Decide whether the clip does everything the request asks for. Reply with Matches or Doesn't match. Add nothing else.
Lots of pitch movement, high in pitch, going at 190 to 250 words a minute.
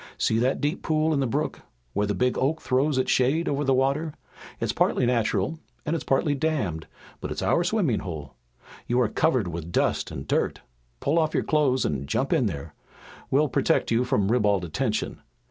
Doesn't match